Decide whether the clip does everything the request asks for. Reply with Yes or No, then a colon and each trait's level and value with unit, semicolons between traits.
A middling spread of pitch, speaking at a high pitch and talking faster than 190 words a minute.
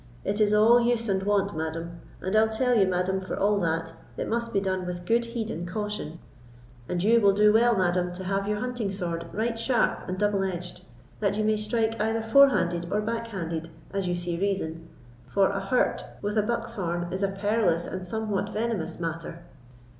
Yes: average, 3.7 semitones; high, 200 Hz; fast, 205 wpm